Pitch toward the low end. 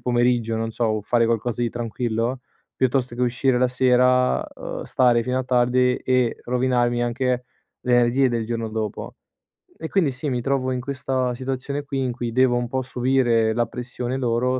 Yes: low, 125 Hz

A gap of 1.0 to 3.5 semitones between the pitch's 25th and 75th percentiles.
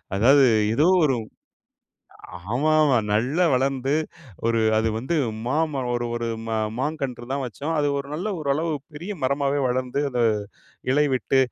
Yes: average, 3.1 semitones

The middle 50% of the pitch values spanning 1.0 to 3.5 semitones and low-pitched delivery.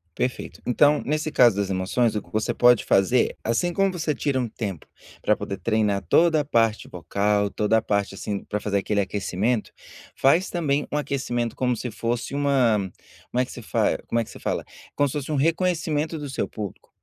No: wide, 5.6 semitones; low, 120 Hz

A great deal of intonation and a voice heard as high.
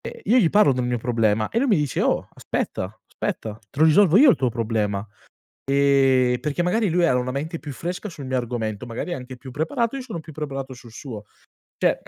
No: wide, 5.9 semitones; low, 135 Hz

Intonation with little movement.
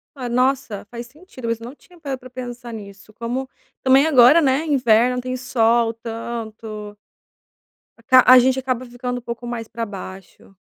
Yes: narrow, 2.1 semitones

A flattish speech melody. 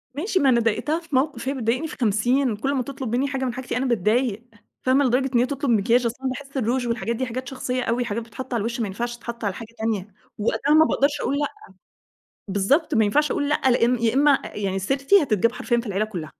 No: average, 3.2 semitones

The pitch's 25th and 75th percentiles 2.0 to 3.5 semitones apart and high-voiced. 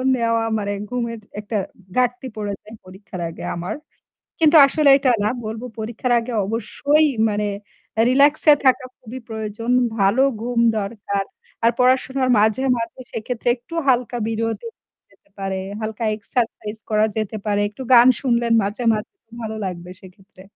Yes: average, 3.1 semitones; high, 225 Hz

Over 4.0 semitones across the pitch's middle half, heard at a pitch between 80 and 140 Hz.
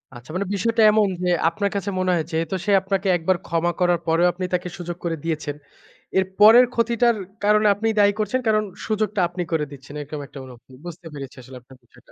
No: average, 4.5 semitones; medium, 180 Hz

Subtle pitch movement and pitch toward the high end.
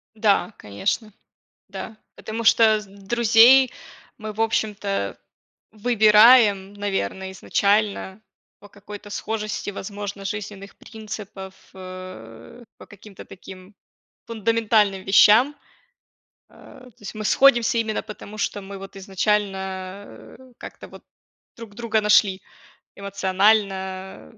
Yes: narrow, 2.2 semitones; high, 205 Hz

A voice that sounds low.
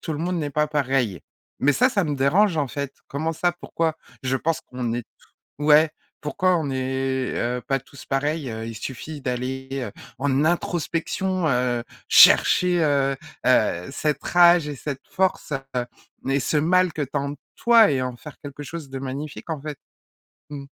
No: medium, 145 Hz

